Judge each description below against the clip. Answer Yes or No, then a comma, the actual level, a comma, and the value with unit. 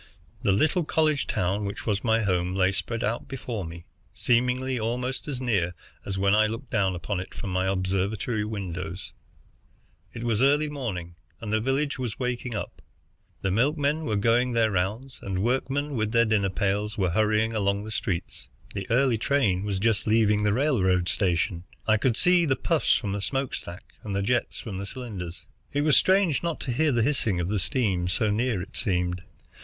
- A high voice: No, low, 110 Hz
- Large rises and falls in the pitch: No, average, 4.6 semitones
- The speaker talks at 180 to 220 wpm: Yes, average, 190 wpm